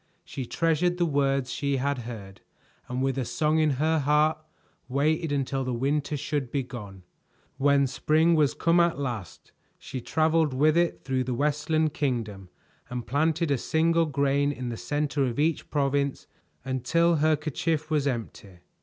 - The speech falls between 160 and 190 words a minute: Yes, average, 165 wpm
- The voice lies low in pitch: No, medium, 145 Hz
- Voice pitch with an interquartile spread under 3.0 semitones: No, average, 3.3 semitones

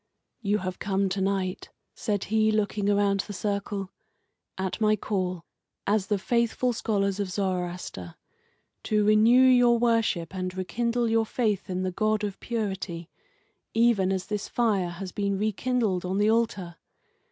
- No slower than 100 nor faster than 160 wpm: Yes, average, 150 wpm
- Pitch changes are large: No, average, 2.8 semitones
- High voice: Yes, high, 200 Hz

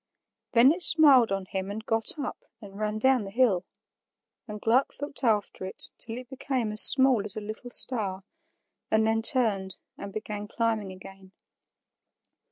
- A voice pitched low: No, high, 220 Hz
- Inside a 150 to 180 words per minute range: Yes, average, 165 wpm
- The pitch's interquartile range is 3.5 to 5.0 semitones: Yes, average, 3.9 semitones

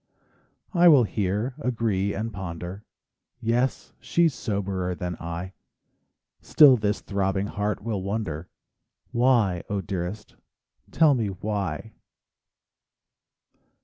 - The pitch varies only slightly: No, average, 3.7 semitones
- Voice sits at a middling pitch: No, low, 100 Hz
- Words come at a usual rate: No, slow, 100 wpm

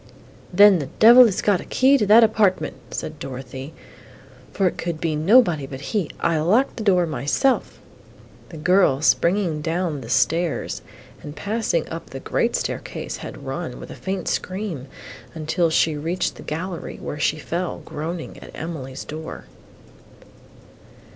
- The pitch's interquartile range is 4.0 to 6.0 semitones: Yes, average, 4.6 semitones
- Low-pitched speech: No, medium, 170 Hz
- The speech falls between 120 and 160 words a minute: Yes, average, 155 wpm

